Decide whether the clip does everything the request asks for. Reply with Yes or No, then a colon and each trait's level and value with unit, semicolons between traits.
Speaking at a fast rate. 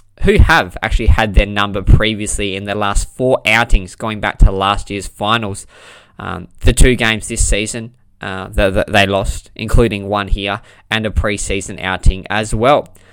No: average, 175 wpm